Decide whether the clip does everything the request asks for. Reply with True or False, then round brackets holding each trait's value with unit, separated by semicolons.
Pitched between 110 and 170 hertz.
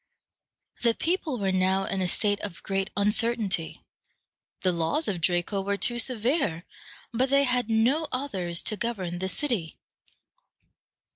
False (205 Hz)